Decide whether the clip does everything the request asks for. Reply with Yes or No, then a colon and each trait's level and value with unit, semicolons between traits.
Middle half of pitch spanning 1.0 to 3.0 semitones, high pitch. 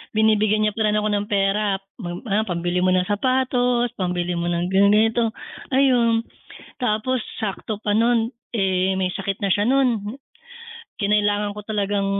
Yes: narrow, 2.6 semitones; high, 210 Hz